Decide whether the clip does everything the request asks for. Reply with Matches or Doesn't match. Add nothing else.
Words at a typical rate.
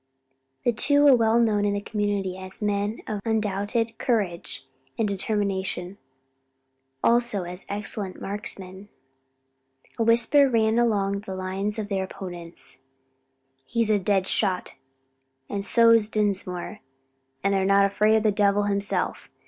Doesn't match